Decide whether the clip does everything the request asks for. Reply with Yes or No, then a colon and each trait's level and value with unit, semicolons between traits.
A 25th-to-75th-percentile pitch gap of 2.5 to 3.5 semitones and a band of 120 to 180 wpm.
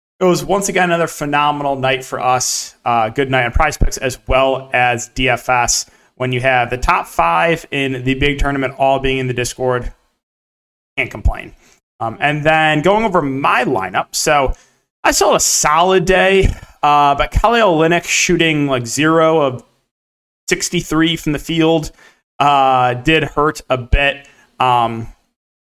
No: average, 4.0 semitones; average, 155 wpm